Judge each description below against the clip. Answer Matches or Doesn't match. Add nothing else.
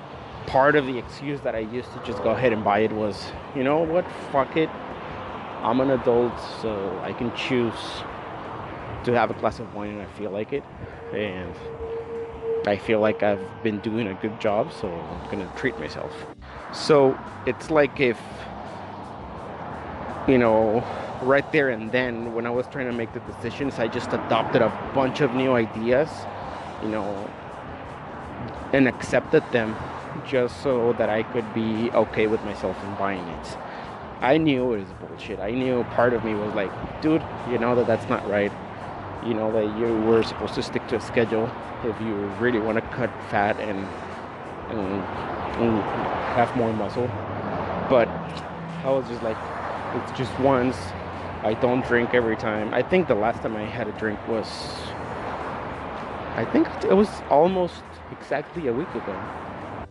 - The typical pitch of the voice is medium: Doesn't match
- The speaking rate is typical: Matches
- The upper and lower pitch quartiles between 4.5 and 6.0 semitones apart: Doesn't match